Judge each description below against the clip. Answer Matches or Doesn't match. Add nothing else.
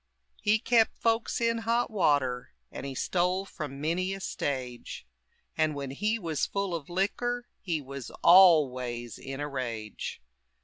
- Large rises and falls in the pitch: Matches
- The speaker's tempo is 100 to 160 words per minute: Matches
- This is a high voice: Doesn't match